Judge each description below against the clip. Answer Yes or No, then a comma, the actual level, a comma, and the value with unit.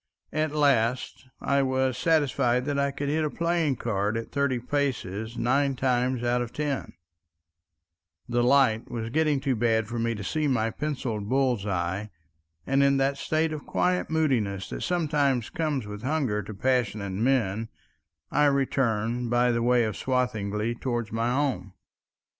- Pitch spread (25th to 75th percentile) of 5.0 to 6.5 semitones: No, average, 3.8 semitones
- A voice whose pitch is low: Yes, low, 125 Hz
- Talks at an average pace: Yes, average, 160 wpm